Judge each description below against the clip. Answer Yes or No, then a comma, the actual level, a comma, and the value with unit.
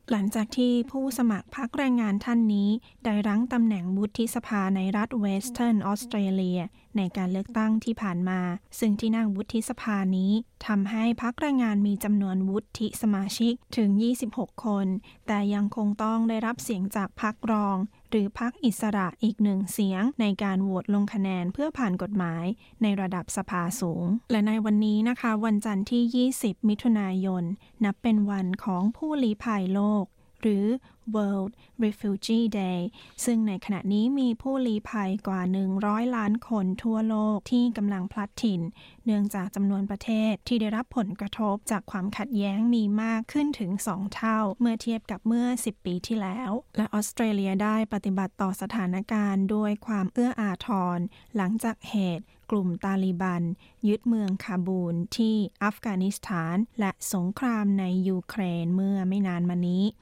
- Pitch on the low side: No, high, 210 Hz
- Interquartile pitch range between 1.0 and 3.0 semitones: Yes, narrow, 2.6 semitones